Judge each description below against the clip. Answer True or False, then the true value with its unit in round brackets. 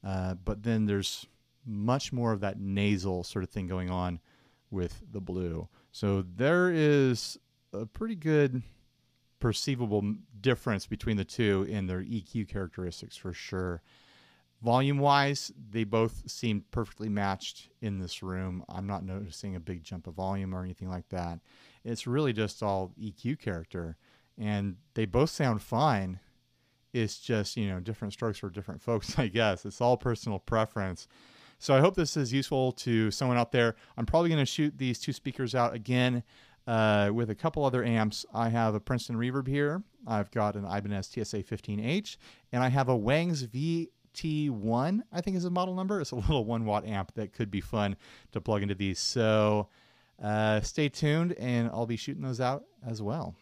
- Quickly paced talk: False (175 wpm)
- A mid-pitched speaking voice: False (110 Hz)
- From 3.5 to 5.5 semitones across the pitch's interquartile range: True (4.4 semitones)